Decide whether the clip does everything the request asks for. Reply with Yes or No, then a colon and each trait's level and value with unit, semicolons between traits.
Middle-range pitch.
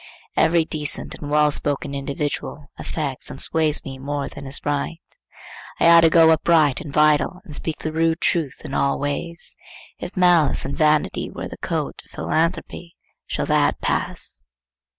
Yes: medium, 150 Hz